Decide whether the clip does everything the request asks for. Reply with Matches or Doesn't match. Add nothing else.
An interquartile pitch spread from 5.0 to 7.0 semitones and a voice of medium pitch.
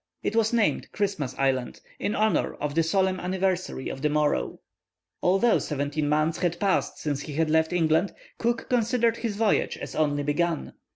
Matches